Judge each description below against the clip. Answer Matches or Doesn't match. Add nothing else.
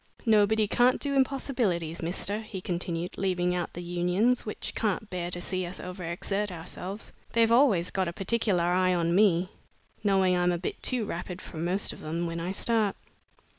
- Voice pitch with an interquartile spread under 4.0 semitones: Matches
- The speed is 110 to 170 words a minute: Doesn't match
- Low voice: Doesn't match